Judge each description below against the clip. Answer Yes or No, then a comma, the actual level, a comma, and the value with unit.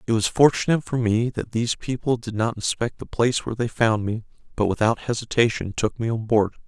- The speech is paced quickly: Yes, fast, 215 wpm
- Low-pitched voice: Yes, low, 115 Hz